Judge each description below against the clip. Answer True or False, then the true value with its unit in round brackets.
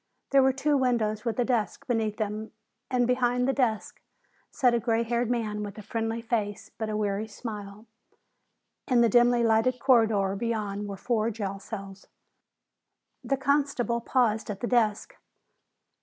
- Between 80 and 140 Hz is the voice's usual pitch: False (225 Hz)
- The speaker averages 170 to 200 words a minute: False (155 wpm)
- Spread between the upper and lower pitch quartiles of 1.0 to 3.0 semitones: True (2.6 semitones)